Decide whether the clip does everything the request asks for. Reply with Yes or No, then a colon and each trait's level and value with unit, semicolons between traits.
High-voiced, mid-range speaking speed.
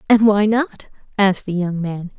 Yes: high, 200 Hz; average, 190 wpm